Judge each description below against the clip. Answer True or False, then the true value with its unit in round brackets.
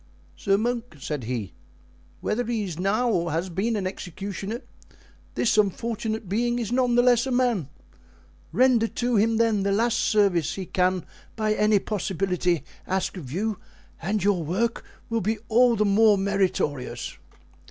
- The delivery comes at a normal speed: True (155 wpm)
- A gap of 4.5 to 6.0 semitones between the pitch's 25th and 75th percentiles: False (3.8 semitones)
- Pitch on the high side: True (210 Hz)